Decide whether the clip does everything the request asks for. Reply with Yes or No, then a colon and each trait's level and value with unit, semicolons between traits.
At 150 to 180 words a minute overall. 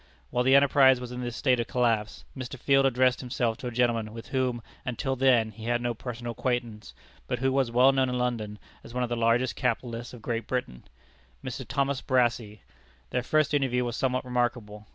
No: average, 200 wpm